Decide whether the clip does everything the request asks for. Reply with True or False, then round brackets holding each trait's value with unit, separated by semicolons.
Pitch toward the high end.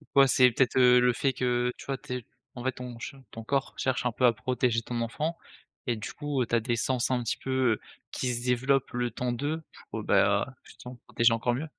False (125 Hz)